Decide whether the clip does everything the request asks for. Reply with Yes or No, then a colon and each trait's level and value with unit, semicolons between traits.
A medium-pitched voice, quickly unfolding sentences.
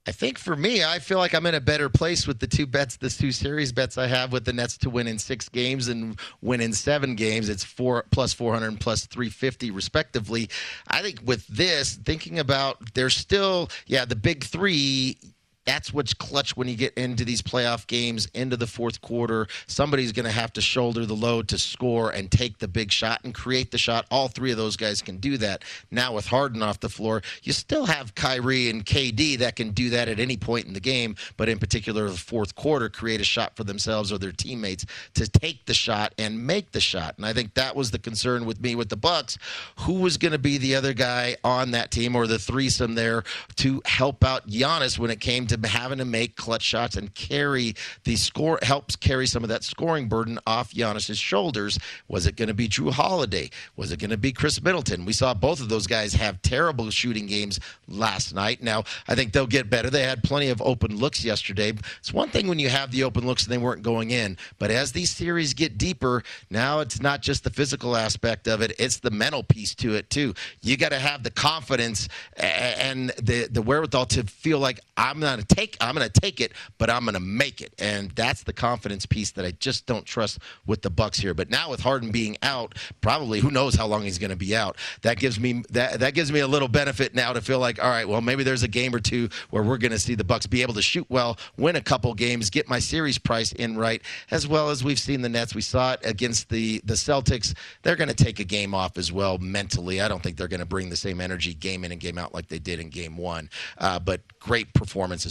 No: low, 120 Hz; fast, 235 wpm